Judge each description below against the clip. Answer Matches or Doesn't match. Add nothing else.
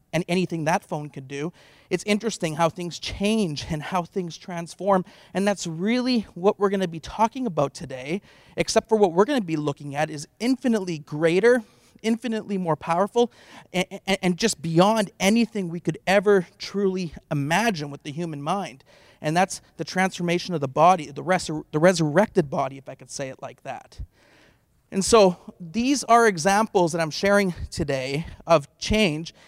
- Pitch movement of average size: Matches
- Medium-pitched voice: Matches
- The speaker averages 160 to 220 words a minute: Matches